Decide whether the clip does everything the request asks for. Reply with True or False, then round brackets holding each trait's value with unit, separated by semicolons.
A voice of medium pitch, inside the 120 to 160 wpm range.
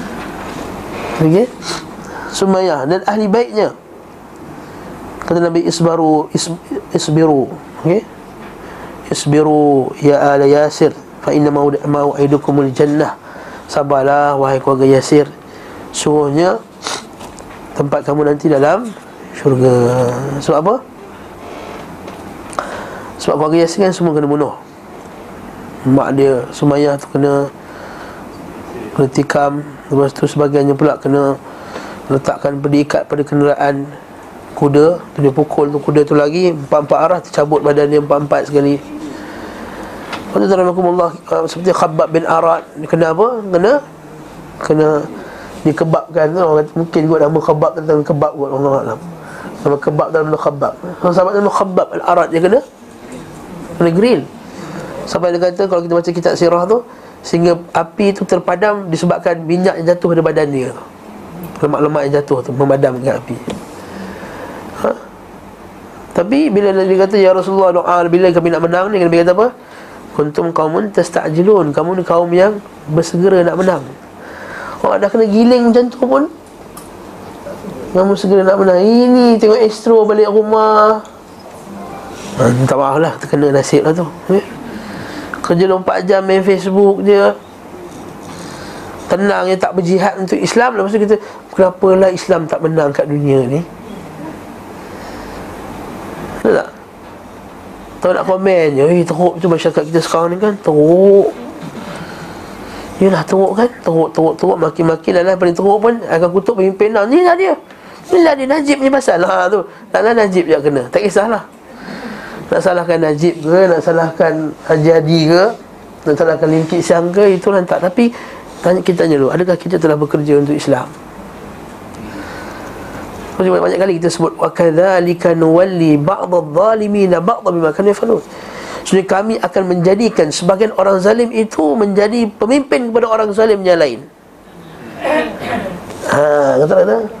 True (170 Hz; 140 wpm)